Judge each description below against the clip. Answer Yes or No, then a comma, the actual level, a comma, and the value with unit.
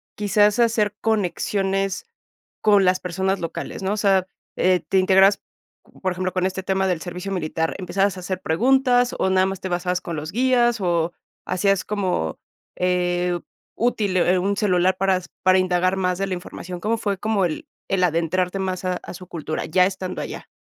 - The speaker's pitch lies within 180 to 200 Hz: Yes, medium, 185 Hz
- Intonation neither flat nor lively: No, narrow, 1.7 semitones